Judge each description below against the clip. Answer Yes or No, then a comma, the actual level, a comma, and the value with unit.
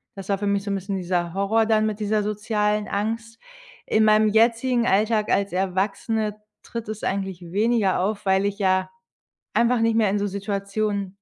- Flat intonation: Yes, narrow, 1.9 semitones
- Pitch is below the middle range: No, high, 210 Hz